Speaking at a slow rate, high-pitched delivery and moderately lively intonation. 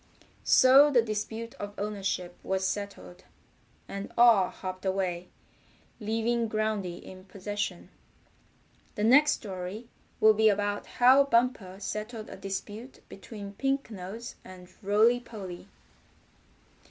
Yes: slow, 115 wpm; high, 210 Hz; average, 3.3 semitones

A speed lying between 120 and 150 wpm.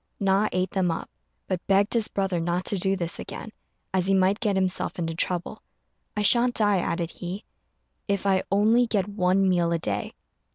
No: average, 190 wpm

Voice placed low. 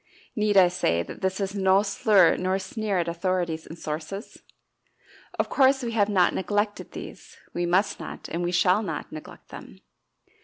No: high, 190 Hz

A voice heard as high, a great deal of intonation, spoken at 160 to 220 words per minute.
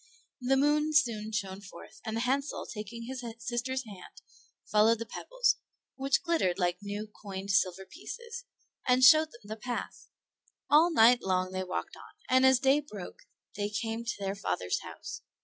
No: high, 230 Hz; average, 4.9 semitones; average, 165 wpm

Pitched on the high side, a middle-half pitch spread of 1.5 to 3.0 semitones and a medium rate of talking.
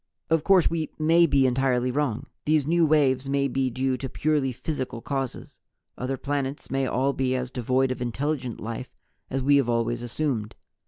No: low, 135 Hz; narrow, 2.4 semitones; average, 175 wpm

